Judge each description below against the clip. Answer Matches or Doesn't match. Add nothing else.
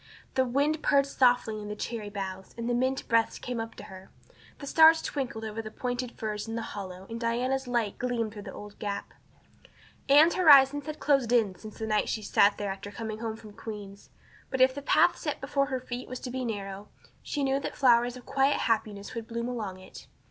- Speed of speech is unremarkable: Doesn't match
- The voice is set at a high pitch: Matches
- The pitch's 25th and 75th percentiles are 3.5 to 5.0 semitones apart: Matches